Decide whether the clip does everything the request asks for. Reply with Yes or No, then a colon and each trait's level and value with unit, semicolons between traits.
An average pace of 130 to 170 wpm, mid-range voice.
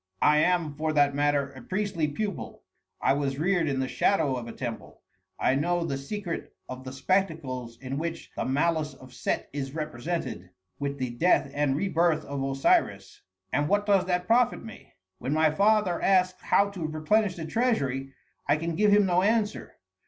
No: average, 180 wpm; medium, 155 Hz